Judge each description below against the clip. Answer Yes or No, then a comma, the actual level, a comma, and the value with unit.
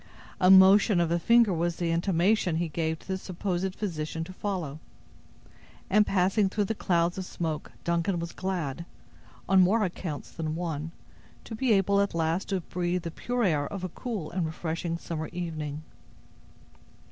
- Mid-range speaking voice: Yes, medium, 175 Hz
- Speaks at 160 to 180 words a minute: Yes, average, 165 wpm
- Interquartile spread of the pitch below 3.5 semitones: Yes, average, 2.8 semitones